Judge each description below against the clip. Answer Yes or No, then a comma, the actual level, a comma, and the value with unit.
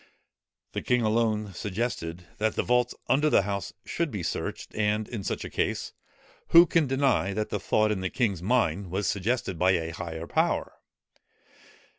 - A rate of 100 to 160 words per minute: No, average, 170 wpm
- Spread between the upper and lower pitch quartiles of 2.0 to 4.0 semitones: No, average, 4.5 semitones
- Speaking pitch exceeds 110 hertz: No, low, 105 Hz